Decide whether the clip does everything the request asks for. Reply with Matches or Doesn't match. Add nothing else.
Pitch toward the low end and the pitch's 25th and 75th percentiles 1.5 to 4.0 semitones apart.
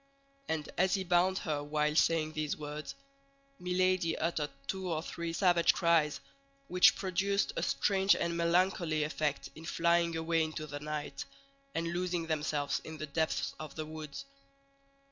Doesn't match